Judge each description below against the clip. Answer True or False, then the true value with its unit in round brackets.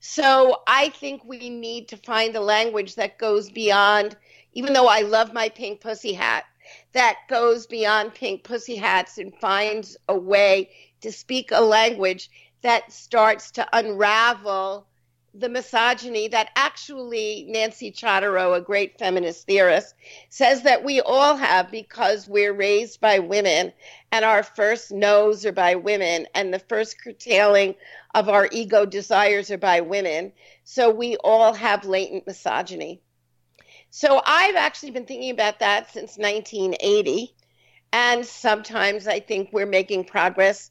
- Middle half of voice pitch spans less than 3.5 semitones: True (2.7 semitones)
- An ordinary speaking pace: True (145 wpm)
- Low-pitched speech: False (215 Hz)